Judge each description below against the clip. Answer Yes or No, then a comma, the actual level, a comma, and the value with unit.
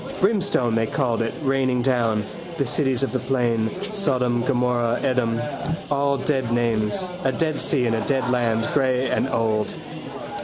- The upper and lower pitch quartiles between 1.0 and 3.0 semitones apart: Yes, average, 2.7 semitones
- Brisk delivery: No, average, 155 wpm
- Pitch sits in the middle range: No, low, 125 Hz